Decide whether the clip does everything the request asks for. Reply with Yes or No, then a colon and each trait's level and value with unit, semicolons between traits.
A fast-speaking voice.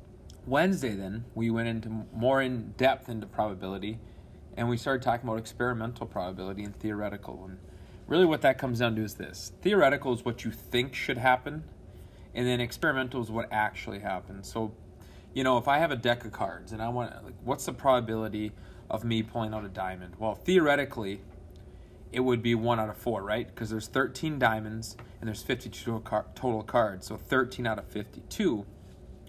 No: average, 180 wpm